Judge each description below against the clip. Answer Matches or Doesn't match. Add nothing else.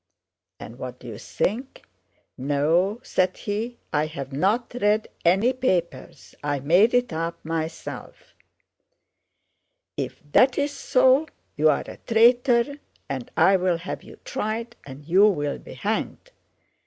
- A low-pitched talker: Doesn't match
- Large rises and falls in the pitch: Matches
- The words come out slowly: Matches